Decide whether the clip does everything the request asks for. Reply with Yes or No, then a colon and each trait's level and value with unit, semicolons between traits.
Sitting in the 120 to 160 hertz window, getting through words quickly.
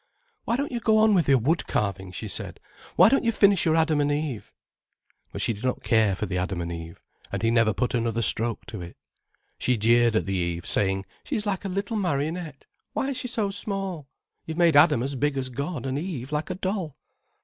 Yes: medium, 140 Hz; fast, 225 wpm